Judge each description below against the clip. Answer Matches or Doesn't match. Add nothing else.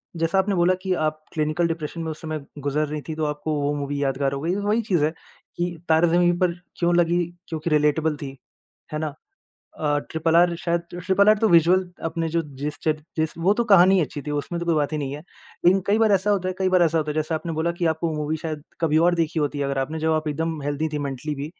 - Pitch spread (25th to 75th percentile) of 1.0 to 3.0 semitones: Matches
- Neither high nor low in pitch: Matches